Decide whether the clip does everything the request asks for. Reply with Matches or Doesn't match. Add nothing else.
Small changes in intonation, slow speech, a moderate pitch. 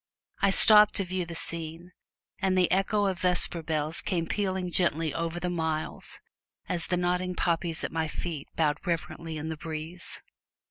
Doesn't match